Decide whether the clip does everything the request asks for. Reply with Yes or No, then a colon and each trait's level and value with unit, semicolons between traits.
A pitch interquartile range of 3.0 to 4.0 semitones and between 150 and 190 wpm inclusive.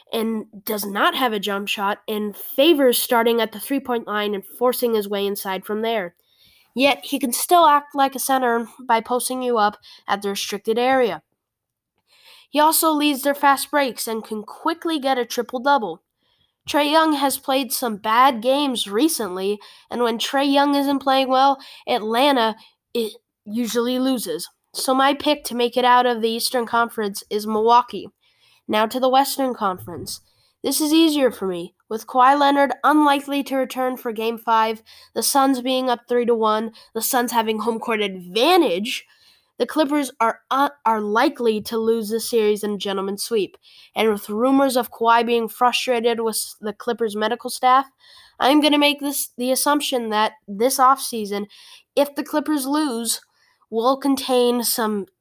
Yes: average, 3.7 semitones; average, 170 wpm